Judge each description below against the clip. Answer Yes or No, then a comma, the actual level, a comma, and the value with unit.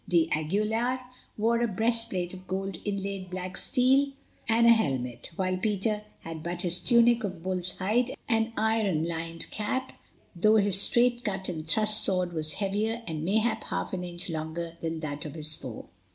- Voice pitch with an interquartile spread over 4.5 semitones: Yes, average, 5.0 semitones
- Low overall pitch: No, high, 190 Hz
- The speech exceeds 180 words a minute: No, average, 165 wpm